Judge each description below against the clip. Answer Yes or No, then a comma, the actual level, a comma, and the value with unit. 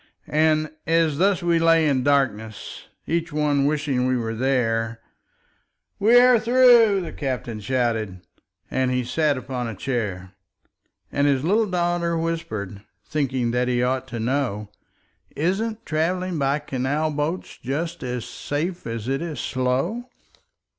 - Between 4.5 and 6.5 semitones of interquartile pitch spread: Yes, average, 5.1 semitones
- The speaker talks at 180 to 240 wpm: No, average, 140 wpm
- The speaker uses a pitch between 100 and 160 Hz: Yes, medium, 140 Hz